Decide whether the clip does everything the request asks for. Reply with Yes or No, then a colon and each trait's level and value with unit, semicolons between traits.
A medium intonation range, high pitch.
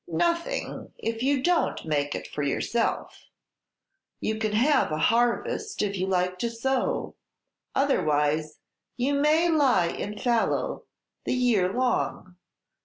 No: wide, 7.1 semitones; high, 230 Hz